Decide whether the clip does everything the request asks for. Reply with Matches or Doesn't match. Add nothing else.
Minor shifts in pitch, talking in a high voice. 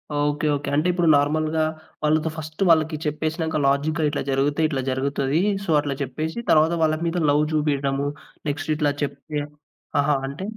Doesn't match